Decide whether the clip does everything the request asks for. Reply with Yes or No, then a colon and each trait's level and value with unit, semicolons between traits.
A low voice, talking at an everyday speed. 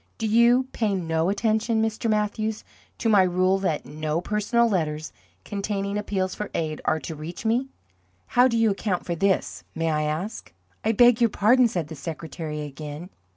No: high, 195 Hz; average, 175 wpm